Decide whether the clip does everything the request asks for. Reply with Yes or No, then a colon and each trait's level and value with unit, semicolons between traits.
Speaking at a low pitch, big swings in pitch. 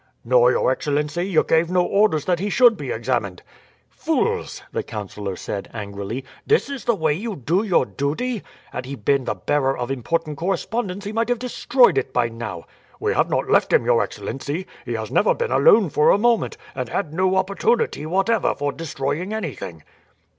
No: medium, 155 Hz; wide, 7.9 semitones